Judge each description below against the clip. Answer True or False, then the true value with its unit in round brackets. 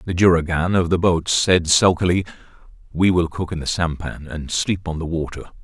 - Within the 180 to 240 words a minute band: True (190 wpm)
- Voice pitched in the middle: False (85 Hz)